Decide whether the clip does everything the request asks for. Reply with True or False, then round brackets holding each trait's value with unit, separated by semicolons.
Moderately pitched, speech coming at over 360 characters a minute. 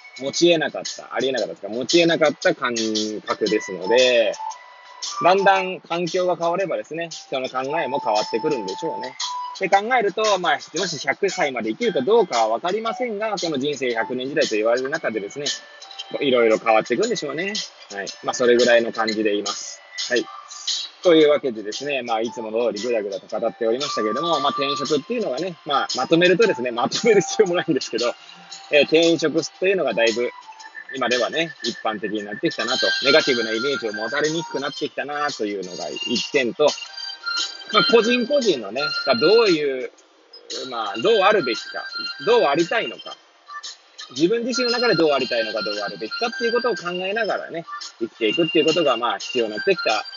True (170 Hz; 420 characters per minute)